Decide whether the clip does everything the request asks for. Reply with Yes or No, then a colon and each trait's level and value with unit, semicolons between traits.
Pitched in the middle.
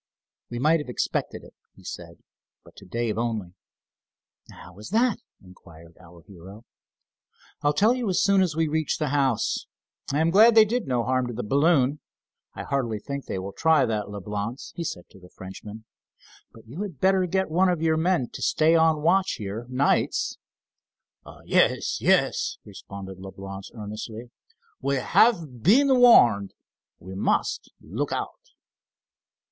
No: low, 130 Hz